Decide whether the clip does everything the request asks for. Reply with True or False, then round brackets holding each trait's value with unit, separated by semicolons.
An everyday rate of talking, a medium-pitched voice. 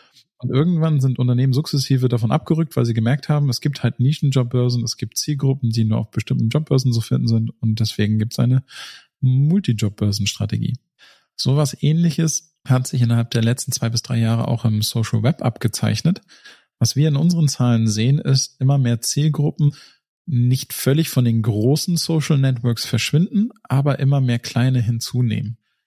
False (165 wpm; 130 Hz)